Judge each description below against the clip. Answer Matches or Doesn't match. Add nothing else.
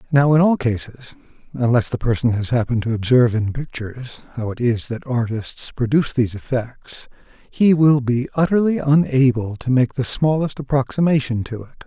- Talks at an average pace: Matches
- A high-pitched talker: Doesn't match